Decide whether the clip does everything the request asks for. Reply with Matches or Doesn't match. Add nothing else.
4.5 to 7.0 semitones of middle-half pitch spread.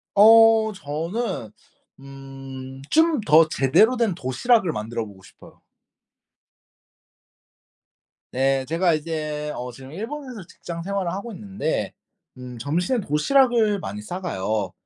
Doesn't match